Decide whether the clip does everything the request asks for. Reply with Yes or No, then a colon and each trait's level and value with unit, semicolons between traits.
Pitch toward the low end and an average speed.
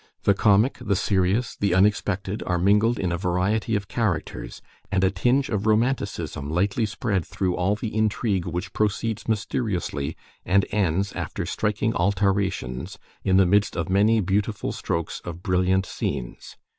Yes: low, 100 Hz; average, 150 wpm